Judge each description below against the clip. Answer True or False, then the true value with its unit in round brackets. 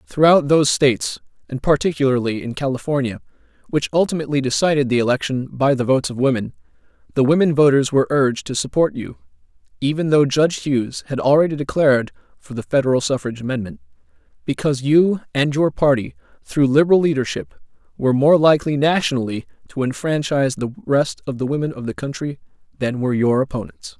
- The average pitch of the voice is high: False (140 Hz)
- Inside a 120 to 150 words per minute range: False (160 wpm)